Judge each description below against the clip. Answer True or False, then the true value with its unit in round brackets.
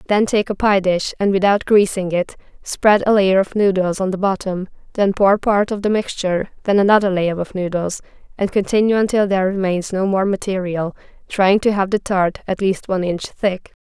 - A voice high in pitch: True (195 Hz)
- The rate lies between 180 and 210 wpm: True (200 wpm)